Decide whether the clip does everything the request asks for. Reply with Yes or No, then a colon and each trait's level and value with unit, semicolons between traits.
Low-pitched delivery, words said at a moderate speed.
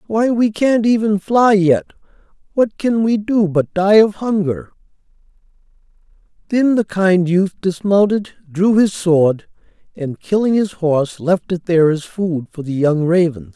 No: high, 190 Hz; average, 155 wpm